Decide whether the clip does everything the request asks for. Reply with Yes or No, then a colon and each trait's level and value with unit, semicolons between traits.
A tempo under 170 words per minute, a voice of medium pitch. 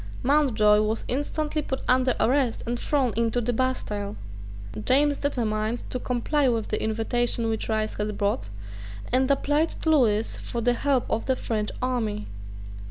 No: average, 155 wpm; high, 240 Hz